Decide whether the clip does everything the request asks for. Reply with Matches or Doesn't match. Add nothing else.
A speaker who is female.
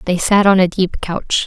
Matches